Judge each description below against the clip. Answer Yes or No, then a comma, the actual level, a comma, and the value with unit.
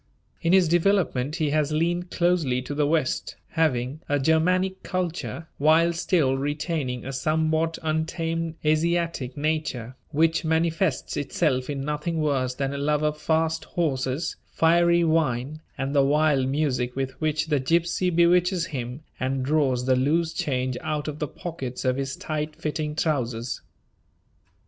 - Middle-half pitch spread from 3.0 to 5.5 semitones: Yes, average, 3.4 semitones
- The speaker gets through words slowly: No, average, 145 wpm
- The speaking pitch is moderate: Yes, medium, 155 Hz